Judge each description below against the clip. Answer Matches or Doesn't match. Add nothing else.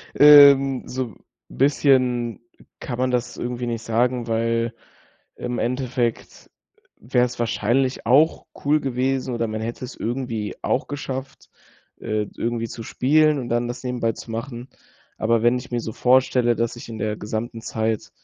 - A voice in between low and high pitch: Doesn't match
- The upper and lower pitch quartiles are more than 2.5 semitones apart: Doesn't match